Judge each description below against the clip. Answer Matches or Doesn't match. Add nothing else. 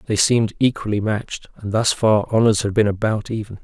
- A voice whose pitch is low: Matches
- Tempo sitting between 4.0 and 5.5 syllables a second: Doesn't match